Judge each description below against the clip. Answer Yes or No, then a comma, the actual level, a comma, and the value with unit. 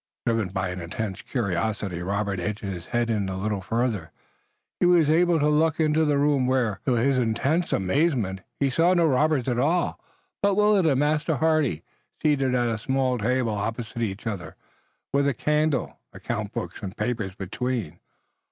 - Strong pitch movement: Yes, wide, 6.6 semitones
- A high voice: No, low, 125 Hz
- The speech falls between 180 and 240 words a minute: No, average, 170 wpm